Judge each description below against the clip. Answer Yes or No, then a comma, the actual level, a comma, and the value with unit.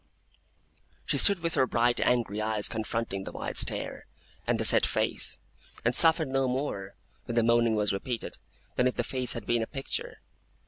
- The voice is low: Yes, low, 120 Hz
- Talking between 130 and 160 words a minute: No, average, 180 wpm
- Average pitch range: Yes, average, 3.0 semitones